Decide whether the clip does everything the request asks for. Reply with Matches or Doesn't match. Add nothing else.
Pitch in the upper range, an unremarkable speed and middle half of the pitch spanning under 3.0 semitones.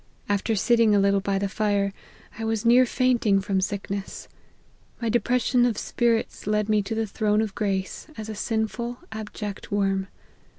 Matches